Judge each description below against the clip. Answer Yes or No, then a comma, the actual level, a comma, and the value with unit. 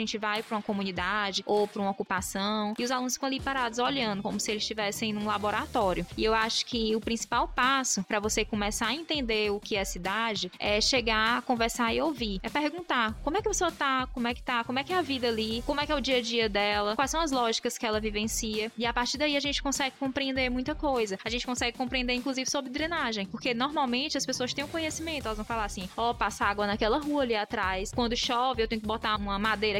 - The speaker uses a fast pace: Yes, fast, 250 wpm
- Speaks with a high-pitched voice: Yes, high, 235 Hz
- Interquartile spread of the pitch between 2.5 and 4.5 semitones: Yes, average, 3.9 semitones